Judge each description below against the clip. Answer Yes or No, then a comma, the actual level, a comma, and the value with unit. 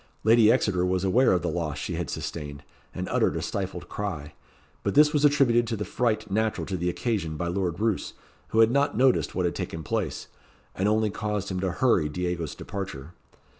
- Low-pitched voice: Yes, very low, 95 Hz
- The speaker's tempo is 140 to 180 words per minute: No, average, 200 wpm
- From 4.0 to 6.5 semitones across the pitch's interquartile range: Yes, average, 4.5 semitones